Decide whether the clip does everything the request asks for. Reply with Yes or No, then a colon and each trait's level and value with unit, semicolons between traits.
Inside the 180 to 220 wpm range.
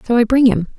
No: fast, 305 wpm